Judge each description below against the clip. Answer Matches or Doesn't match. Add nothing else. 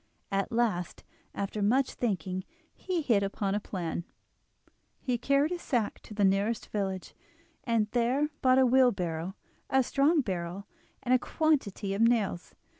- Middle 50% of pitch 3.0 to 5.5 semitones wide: Matches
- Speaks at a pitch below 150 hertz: Doesn't match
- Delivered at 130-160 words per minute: Matches